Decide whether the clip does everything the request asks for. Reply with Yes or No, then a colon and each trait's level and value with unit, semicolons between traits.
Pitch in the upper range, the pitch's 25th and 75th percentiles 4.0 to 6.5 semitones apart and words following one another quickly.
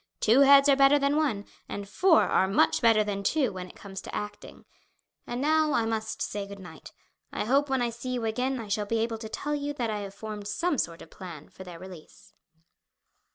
Yes: high, 225 Hz; wide, 5.4 semitones; fast, 225 wpm